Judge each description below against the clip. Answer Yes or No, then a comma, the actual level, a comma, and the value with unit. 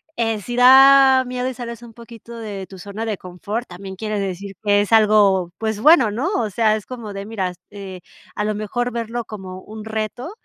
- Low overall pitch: No, high, 215 Hz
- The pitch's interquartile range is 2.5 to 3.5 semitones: Yes, average, 3.0 semitones